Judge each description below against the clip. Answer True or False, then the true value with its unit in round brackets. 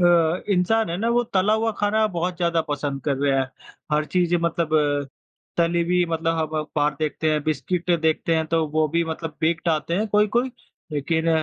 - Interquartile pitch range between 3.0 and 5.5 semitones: False (2.5 semitones)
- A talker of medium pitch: True (165 Hz)